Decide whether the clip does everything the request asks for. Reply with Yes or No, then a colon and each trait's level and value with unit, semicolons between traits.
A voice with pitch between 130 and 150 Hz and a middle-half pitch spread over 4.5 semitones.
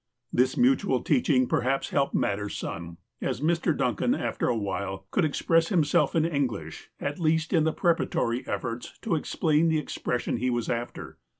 Yes: medium, 140 Hz; wide, 5.5 semitones